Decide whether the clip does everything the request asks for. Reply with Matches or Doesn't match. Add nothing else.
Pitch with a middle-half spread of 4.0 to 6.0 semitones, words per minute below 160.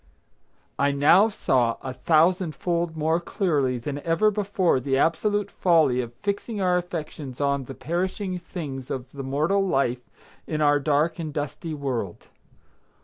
Matches